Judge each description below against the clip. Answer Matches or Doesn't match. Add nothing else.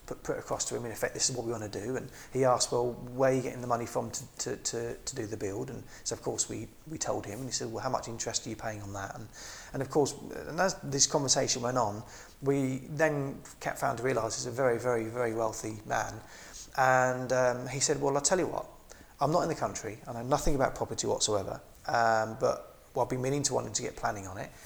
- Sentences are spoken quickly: Matches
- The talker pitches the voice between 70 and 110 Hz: Doesn't match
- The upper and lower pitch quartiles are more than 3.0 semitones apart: Doesn't match